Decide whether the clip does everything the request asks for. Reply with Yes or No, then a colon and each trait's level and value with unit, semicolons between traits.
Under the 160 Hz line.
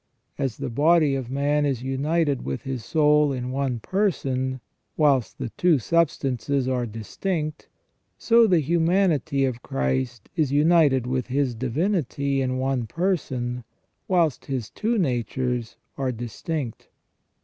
Yes: low, 135 Hz